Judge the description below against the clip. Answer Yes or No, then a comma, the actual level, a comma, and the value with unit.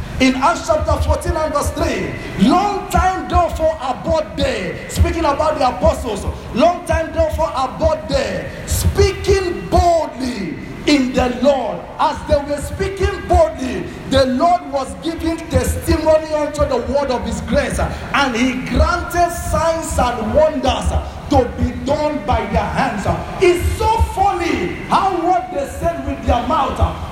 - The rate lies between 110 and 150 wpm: Yes, average, 140 wpm